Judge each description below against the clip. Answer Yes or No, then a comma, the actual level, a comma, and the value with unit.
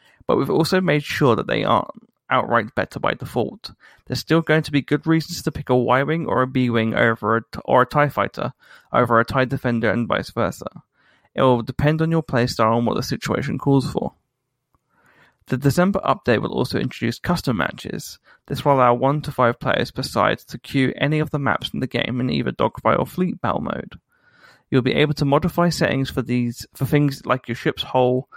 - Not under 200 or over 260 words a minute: Yes, fast, 205 wpm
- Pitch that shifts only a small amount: No, average, 3.4 semitones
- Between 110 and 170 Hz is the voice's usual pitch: Yes, low, 135 Hz